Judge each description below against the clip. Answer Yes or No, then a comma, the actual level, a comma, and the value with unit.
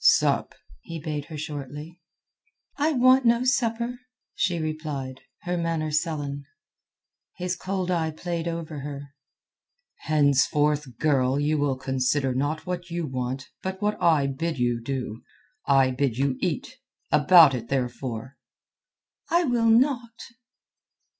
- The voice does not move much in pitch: No, average, 4.7 semitones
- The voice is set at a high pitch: No, medium, 150 Hz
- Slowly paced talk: Yes, slow, 125 wpm